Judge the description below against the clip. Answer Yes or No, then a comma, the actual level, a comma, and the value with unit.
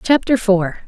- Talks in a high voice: Yes, high, 210 Hz